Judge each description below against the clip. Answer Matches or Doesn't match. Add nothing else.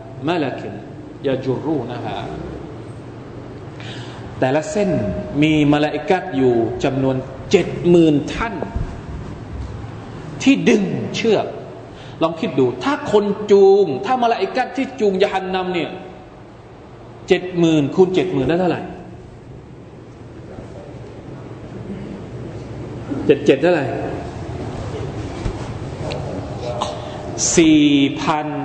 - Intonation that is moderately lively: Doesn't match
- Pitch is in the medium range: Matches